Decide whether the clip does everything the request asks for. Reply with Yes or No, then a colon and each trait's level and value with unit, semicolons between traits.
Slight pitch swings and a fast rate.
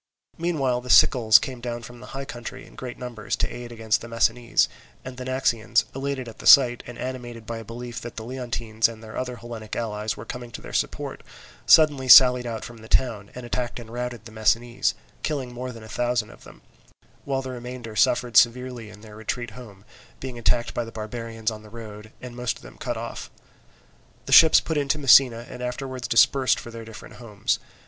Yes: narrow, 1.9 semitones; fast, 210 wpm